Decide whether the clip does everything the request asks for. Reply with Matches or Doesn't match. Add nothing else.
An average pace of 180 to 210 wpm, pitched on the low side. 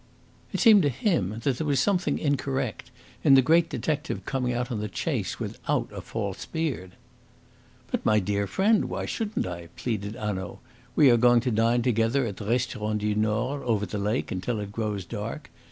Matches